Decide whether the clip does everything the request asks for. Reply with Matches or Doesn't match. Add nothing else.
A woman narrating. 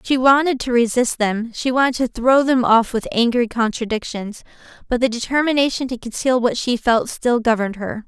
Matches